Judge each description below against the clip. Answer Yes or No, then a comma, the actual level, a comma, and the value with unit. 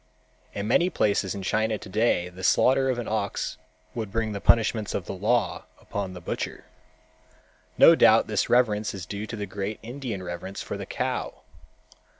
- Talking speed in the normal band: Yes, average, 170 wpm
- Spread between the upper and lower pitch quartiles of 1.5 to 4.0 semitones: Yes, average, 2.8 semitones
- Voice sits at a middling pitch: No, low, 105 Hz